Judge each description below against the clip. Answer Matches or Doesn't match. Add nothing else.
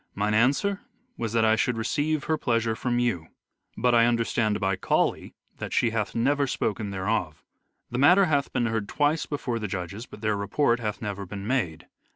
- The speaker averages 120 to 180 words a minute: Doesn't match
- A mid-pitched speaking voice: Doesn't match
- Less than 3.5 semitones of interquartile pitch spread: Doesn't match